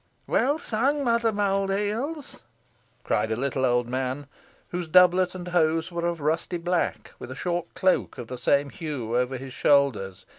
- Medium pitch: Yes, medium, 170 Hz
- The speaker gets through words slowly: No, average, 170 wpm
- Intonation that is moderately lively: No, wide, 6.7 semitones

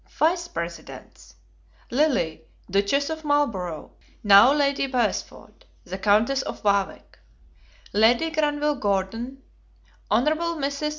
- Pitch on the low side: No, very high, 260 Hz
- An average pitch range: No, wide, 6.7 semitones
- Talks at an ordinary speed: No, slow, 105 wpm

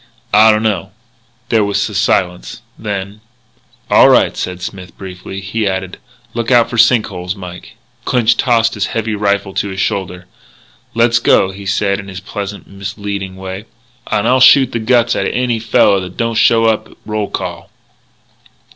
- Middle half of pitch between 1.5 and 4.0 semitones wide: Yes, average, 3.1 semitones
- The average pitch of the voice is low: Yes, low, 105 Hz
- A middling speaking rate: Yes, average, 170 wpm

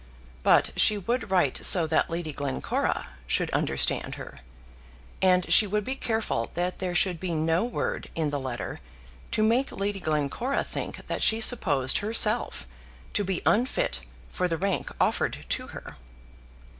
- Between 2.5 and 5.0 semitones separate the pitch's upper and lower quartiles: No, wide, 5.4 semitones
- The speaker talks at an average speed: Yes, average, 155 wpm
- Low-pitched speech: No, medium, 185 Hz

